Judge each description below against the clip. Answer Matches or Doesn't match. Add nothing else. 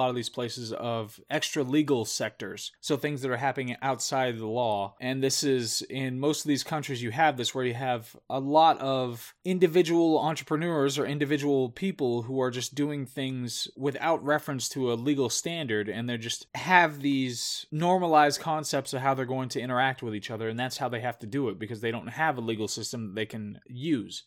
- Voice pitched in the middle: Doesn't match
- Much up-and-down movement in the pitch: Doesn't match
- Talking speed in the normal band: Doesn't match